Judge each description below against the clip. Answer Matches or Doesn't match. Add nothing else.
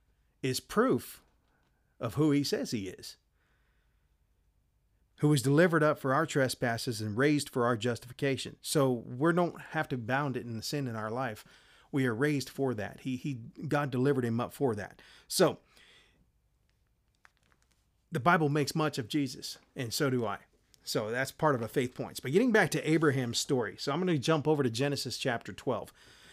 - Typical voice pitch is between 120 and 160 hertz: Matches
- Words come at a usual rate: Matches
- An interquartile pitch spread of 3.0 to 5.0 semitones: Matches